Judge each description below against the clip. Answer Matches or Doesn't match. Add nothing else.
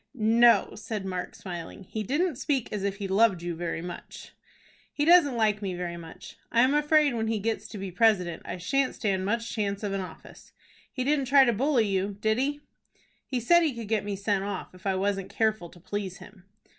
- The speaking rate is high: Matches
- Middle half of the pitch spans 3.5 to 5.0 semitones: Matches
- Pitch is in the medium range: Doesn't match